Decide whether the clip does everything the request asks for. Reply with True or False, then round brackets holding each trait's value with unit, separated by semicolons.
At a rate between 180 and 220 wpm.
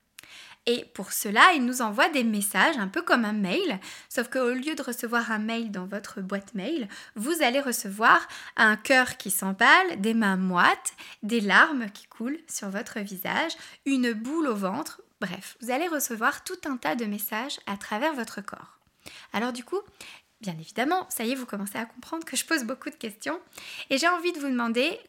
True (195 wpm)